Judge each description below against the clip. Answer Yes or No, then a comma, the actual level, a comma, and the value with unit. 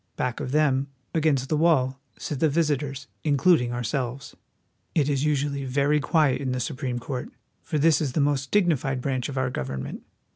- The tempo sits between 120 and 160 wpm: No, average, 175 wpm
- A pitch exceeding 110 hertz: Yes, medium, 140 Hz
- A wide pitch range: No, average, 2.7 semitones